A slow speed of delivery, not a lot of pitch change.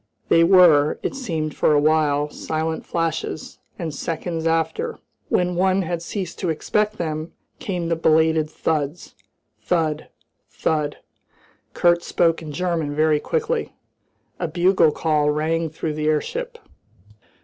Yes: slow, 130 wpm; narrow, 2.1 semitones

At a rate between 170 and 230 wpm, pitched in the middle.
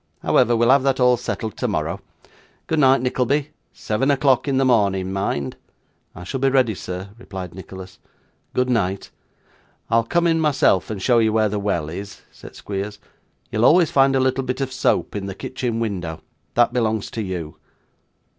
No: average, 175 wpm; low, 115 Hz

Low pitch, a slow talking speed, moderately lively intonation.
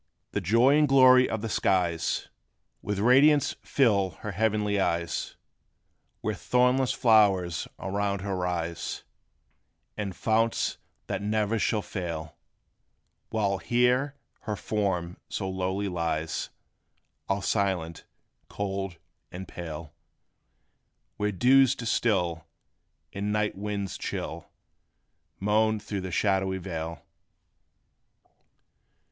Yes: low, 100 Hz; slow, 100 wpm; average, 3.6 semitones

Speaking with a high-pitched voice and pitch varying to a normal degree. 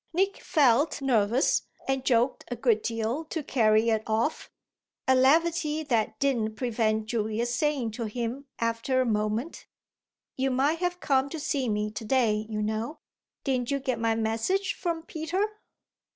Yes: very high, 250 Hz; average, 4.7 semitones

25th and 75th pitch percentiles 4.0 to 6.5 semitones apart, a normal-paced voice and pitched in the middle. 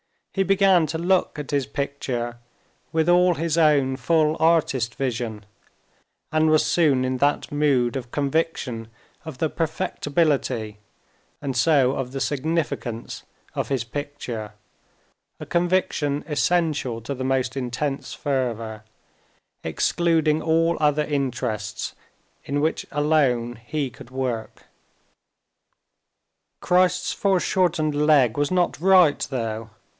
No: average, 4.3 semitones; slow, 110 wpm; medium, 145 Hz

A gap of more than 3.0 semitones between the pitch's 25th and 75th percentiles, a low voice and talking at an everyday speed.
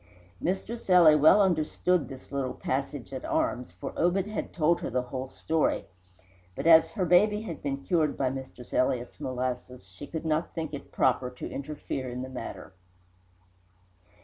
No: average, 4.9 semitones; medium, 145 Hz; average, 165 wpm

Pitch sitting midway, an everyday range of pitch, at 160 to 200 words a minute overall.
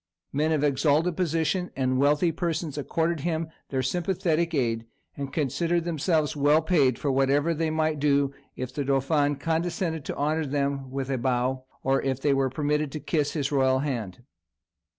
Yes: medium, 145 Hz; average, 3.1 semitones; average, 170 wpm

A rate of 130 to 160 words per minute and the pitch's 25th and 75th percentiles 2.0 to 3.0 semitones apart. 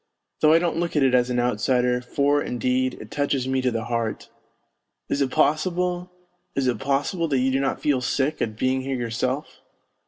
No: average, 195 wpm; average, 2.7 semitones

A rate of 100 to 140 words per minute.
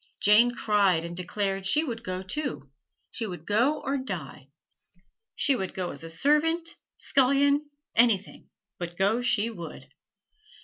Yes: slow, 135 wpm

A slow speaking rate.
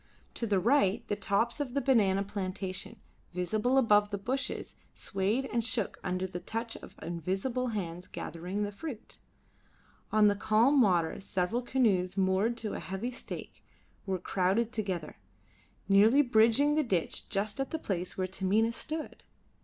No: average, 155 wpm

